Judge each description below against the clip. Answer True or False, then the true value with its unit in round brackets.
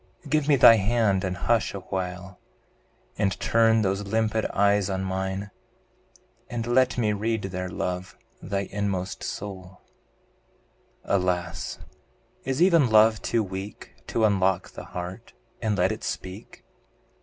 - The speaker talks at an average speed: False (130 wpm)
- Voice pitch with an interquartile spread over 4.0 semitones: False (3.1 semitones)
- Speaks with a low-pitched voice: True (100 Hz)